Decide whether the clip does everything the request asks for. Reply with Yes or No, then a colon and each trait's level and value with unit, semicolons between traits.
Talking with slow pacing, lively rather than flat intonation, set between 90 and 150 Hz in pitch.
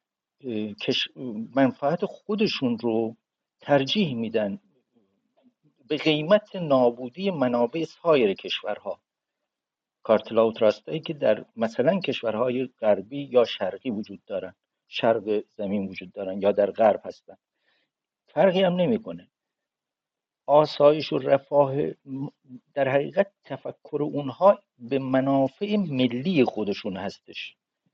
Yes: slow, 100 wpm; wide, 5.8 semitones; low, 135 Hz